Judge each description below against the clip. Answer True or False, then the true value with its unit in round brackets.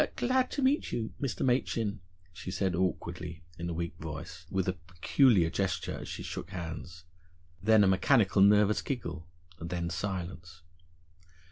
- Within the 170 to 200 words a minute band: False (150 wpm)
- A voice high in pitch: False (95 Hz)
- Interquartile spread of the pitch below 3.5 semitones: False (4.0 semitones)